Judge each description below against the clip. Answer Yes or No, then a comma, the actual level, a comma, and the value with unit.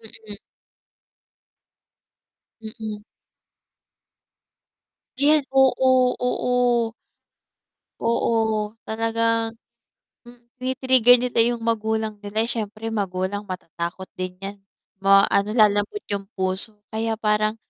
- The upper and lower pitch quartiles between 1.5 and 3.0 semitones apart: Yes, narrow, 2.6 semitones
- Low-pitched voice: No, high, 220 Hz